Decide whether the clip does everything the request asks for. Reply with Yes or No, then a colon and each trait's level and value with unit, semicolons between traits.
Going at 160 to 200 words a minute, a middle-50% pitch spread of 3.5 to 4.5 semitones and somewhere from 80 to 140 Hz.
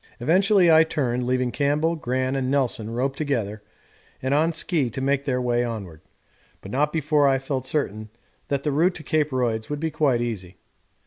Yes: average, 185 wpm; average, 3.9 semitones; low, 135 Hz